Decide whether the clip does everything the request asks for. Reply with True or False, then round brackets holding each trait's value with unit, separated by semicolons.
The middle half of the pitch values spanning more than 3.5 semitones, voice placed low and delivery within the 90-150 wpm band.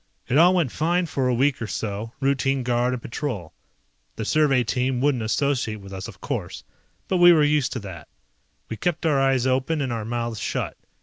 False (4.1 semitones; 130 Hz; 200 wpm)